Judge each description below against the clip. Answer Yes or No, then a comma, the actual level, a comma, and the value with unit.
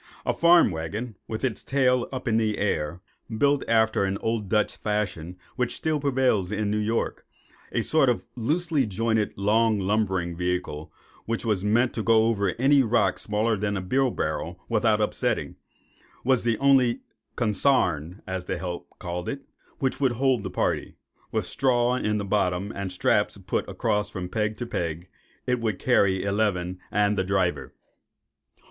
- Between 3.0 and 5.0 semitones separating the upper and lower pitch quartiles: Yes, average, 4.2 semitones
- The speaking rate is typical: Yes, average, 160 wpm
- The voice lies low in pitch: Yes, low, 105 Hz